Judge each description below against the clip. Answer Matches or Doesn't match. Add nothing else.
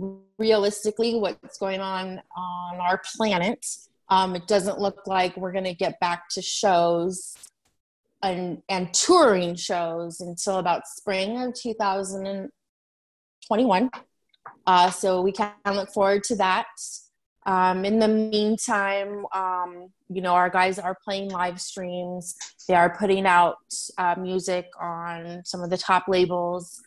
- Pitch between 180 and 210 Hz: Matches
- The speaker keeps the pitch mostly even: Matches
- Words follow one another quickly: Doesn't match